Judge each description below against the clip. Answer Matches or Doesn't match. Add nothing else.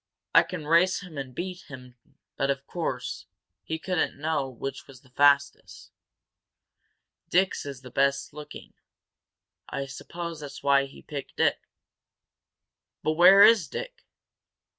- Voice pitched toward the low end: Doesn't match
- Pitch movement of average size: Matches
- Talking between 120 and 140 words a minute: Matches